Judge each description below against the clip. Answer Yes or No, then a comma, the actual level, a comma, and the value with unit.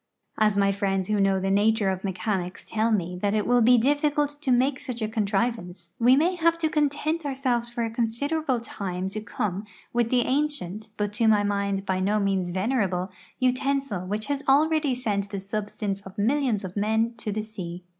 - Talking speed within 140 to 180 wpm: No, average, 200 wpm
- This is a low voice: No, high, 215 Hz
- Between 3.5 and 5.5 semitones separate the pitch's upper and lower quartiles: Yes, average, 4.6 semitones